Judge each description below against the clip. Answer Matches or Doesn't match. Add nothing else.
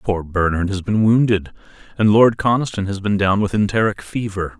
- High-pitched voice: Doesn't match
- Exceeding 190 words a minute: Doesn't match